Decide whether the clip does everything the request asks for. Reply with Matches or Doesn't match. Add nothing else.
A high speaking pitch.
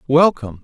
Doesn't match